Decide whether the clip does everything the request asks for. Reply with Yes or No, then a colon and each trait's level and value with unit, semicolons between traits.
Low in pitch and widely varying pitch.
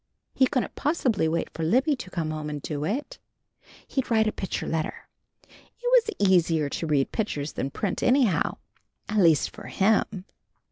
No: high, 190 Hz; wide, 8.1 semitones